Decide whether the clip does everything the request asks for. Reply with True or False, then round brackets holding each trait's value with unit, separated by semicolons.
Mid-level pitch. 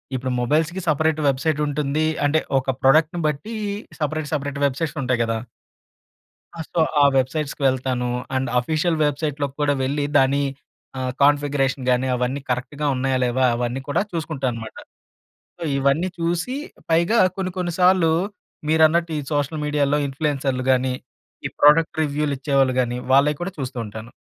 True (145 Hz)